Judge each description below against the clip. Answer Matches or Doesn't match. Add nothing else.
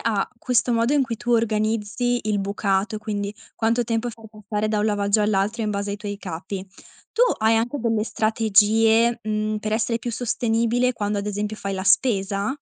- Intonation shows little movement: Matches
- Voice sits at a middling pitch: Doesn't match